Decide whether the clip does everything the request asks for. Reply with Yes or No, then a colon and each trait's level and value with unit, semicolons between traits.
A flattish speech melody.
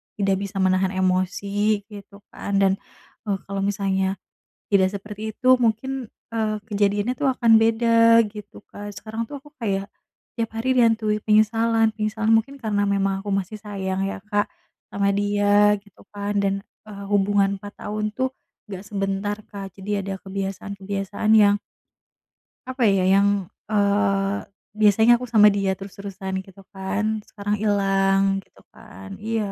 Yes: narrow, 1.7 semitones